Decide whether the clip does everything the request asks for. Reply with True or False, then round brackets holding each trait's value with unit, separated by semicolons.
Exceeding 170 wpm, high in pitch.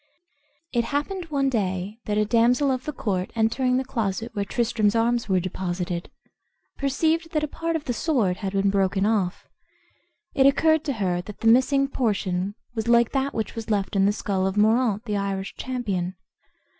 True (180 wpm; 225 Hz)